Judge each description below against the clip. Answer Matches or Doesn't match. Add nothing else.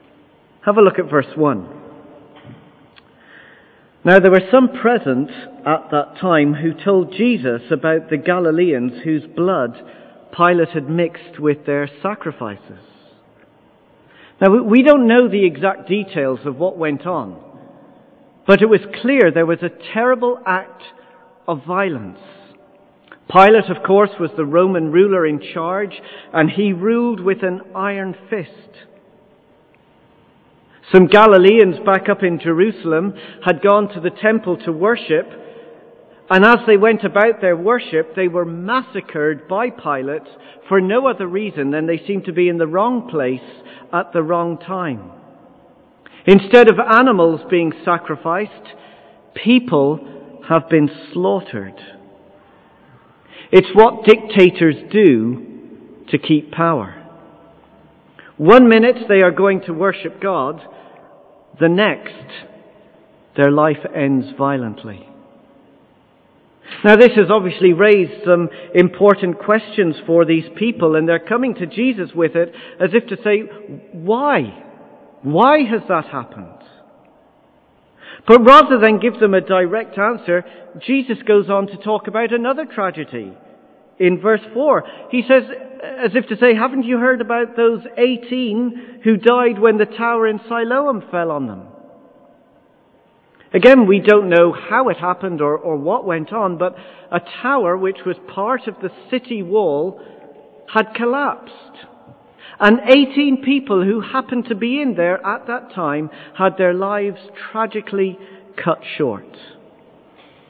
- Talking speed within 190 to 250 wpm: Doesn't match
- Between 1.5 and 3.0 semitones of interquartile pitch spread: Doesn't match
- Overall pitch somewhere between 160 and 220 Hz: Matches